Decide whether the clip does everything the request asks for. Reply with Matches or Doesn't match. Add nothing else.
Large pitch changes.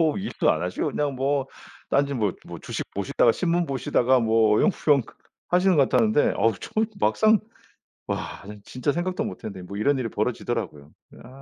Matches